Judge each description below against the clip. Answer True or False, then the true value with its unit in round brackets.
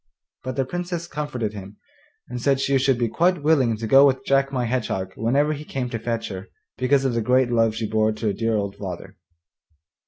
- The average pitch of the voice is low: True (125 Hz)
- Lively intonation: False (3.8 semitones)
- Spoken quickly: True (215 wpm)